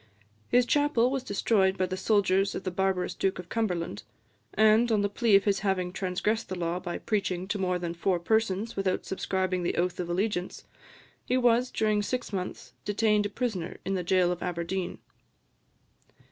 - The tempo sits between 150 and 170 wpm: No, average, 180 wpm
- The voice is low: No, high, 195 Hz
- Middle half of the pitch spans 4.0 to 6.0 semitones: No, average, 3.1 semitones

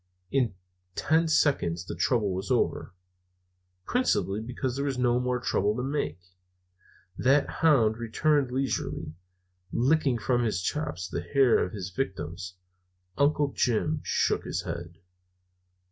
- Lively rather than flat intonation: Yes, wide, 6.3 semitones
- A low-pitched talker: Yes, low, 125 Hz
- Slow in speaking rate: Yes, slow, 130 wpm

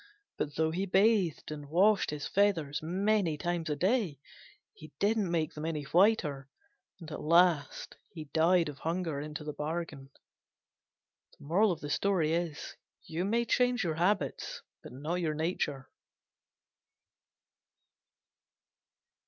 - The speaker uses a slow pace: Yes, slow, 110 wpm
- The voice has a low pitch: No, medium, 165 Hz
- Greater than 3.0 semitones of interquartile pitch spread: Yes, average, 4.1 semitones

